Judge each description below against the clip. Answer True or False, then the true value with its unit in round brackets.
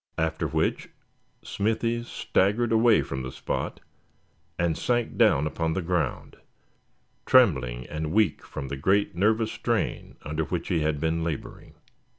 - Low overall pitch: True (85 Hz)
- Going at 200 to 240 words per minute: False (140 wpm)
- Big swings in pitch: True (6.4 semitones)